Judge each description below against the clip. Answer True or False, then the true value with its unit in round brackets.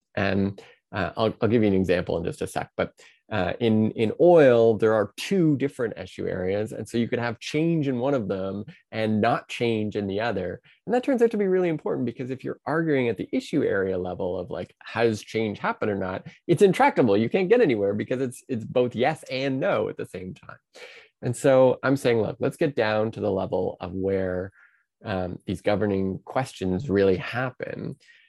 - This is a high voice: False (120 Hz)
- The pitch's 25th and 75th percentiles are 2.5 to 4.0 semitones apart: False (5.3 semitones)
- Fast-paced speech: True (210 wpm)